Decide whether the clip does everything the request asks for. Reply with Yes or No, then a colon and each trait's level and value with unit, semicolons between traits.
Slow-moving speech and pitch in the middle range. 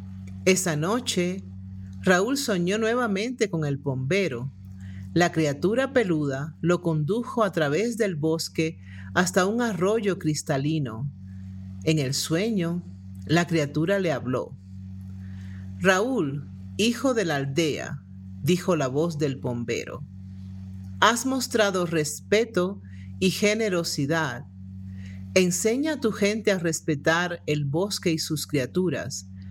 Yes: slow, 110 wpm; medium, 160 Hz